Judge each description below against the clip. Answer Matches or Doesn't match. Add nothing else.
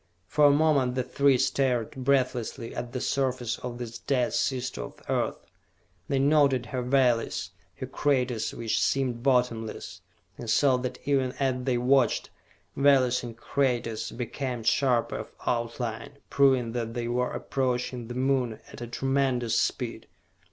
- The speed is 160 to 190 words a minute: Doesn't match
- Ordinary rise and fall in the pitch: Doesn't match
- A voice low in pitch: Matches